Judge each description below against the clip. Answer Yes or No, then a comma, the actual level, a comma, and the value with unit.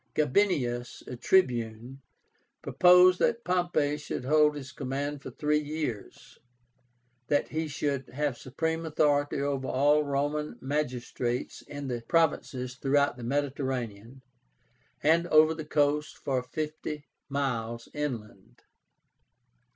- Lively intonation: No, average, 3.0 semitones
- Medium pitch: Yes, medium, 145 Hz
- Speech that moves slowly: Yes, slow, 110 wpm